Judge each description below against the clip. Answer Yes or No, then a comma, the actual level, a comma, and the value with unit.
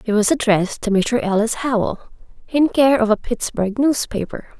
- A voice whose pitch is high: Yes, high, 230 Hz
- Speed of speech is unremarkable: Yes, average, 170 wpm